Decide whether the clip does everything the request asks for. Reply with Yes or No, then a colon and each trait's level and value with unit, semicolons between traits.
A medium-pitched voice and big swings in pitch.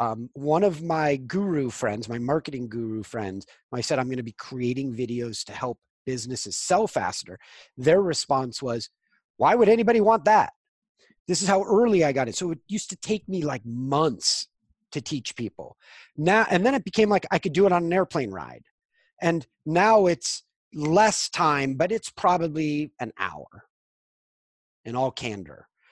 Yes: medium, 155 Hz; wide, 7.8 semitones